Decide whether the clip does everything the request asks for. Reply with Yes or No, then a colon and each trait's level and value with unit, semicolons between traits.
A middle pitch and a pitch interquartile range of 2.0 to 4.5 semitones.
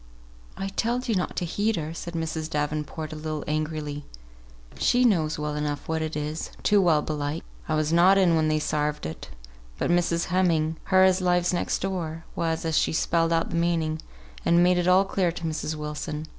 Yes: medium, 160 Hz; narrow, 2.5 semitones